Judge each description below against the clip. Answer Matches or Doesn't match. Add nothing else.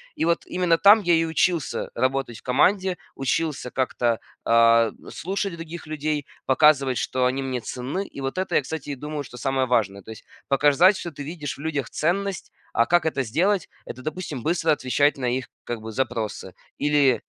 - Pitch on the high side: Doesn't match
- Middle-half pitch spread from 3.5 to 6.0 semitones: Matches